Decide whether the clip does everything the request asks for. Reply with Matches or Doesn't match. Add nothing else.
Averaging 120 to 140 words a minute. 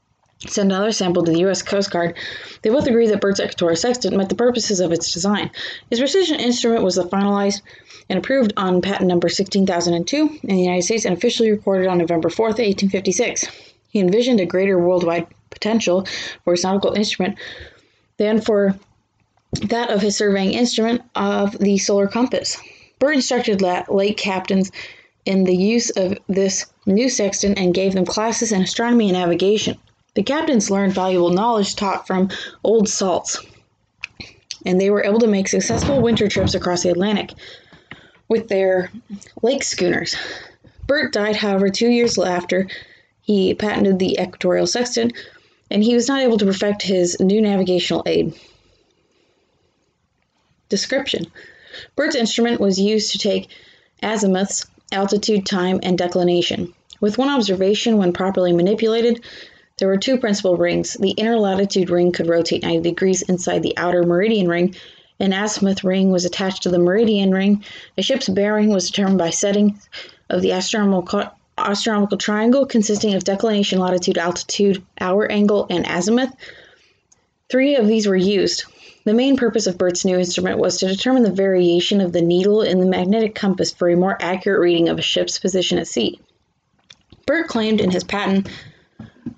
Doesn't match